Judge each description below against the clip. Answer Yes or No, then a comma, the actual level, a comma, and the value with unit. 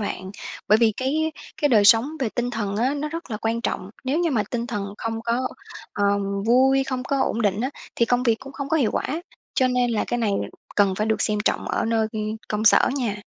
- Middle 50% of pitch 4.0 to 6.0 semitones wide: No, average, 3.5 semitones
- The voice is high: Yes, high, 230 Hz